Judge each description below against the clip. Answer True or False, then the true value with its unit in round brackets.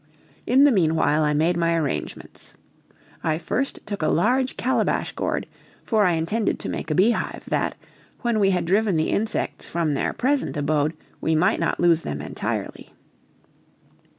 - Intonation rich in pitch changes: True (5.9 semitones)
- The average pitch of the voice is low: False (170 Hz)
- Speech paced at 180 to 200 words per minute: False (160 wpm)